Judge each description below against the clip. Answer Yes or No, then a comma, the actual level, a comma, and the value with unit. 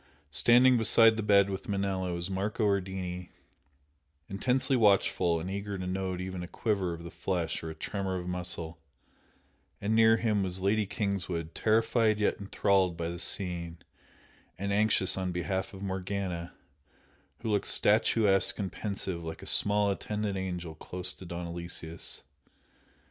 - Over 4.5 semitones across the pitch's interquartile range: No, narrow, 2.6 semitones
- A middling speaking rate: Yes, average, 155 wpm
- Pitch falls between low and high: No, very low, 95 Hz